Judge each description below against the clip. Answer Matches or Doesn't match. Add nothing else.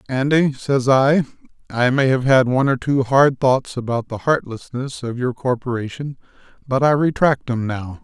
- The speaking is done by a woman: Doesn't match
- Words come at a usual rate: Matches